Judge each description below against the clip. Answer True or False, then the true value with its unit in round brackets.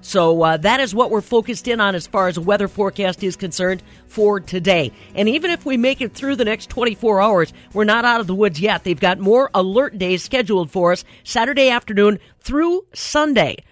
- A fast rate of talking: True (210 wpm)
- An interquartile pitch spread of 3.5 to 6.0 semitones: True (4.6 semitones)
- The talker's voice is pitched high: True (210 Hz)